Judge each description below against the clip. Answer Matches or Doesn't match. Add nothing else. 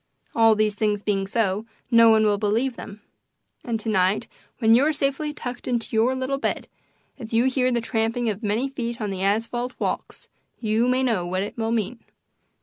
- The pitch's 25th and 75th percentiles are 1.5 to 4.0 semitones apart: Matches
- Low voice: Doesn't match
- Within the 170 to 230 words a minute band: Matches